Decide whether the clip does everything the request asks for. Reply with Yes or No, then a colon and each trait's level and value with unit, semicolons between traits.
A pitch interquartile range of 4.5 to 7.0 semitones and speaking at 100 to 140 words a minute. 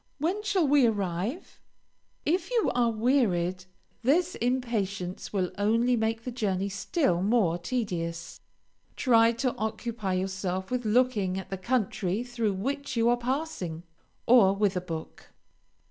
Yes: average, 5.0 semitones; slow, 135 wpm